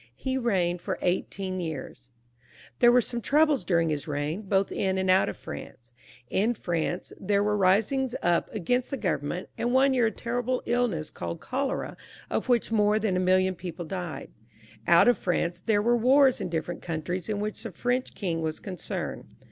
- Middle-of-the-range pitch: No, high, 195 Hz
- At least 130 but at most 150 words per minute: No, average, 185 wpm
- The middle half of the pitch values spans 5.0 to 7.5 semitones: Yes, wide, 5.6 semitones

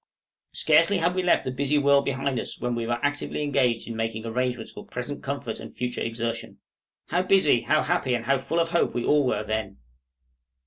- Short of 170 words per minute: No, fast, 205 wpm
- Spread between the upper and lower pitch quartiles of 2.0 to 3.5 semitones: No, average, 4.4 semitones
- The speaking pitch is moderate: No, low, 130 Hz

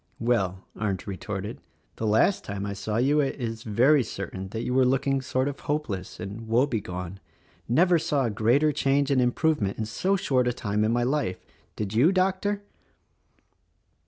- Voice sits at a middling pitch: No, low, 120 Hz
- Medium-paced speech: Yes, average, 185 wpm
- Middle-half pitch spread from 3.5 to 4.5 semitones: No, average, 5.3 semitones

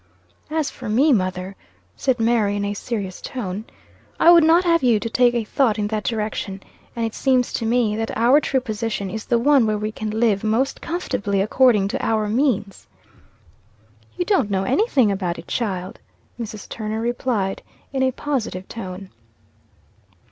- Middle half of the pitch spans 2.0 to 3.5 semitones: No, average, 3.9 semitones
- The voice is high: Yes, high, 225 Hz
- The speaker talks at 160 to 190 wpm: Yes, average, 170 wpm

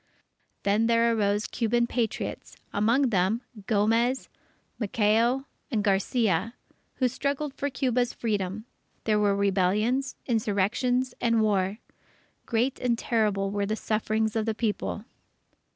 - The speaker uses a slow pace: Yes, slow, 120 wpm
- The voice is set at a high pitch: Yes, high, 225 Hz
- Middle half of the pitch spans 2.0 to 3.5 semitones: Yes, average, 2.8 semitones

